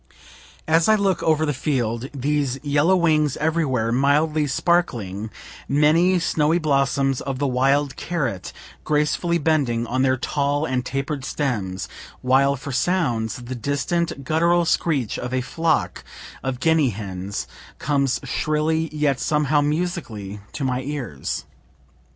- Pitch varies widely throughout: No, average, 3.7 semitones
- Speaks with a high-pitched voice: No, medium, 140 Hz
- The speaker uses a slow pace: Yes, slow, 130 wpm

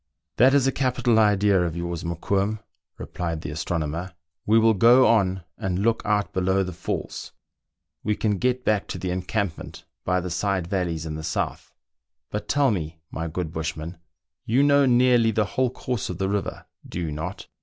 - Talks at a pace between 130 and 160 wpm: No, average, 185 wpm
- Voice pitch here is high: No, very low, 95 Hz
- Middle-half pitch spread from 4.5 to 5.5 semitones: Yes, average, 4.9 semitones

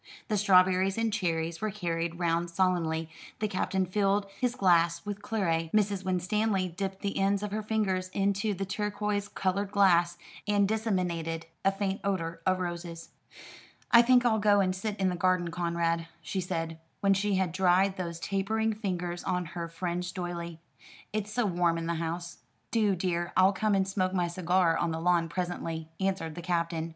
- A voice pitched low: No, medium, 185 Hz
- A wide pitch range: No, average, 2.8 semitones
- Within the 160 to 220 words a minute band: Yes, average, 175 wpm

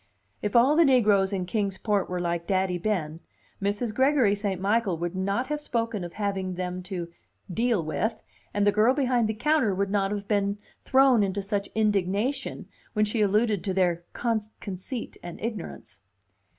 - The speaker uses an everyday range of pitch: Yes, average, 3.4 semitones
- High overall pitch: Yes, high, 205 Hz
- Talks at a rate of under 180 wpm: Yes, average, 170 wpm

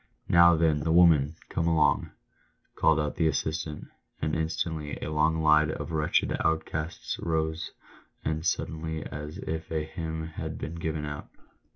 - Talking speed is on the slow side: No, average, 160 wpm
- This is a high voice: No, very low, 80 Hz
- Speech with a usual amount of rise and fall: No, narrow, 1.0 semitones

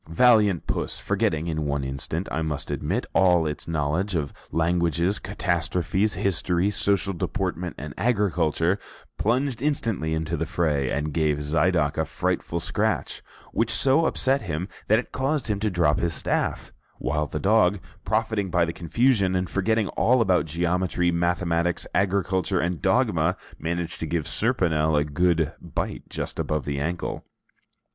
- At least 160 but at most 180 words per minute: No, average, 150 wpm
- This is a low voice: Yes, very low, 85 Hz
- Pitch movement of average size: Yes, average, 4.0 semitones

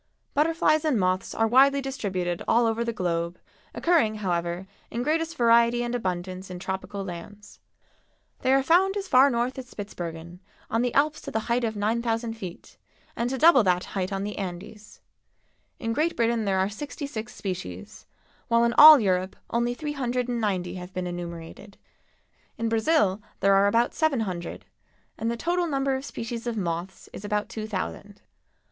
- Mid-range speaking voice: No, high, 225 Hz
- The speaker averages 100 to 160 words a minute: No, average, 175 wpm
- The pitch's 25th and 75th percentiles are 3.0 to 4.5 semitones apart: No, average, 5.0 semitones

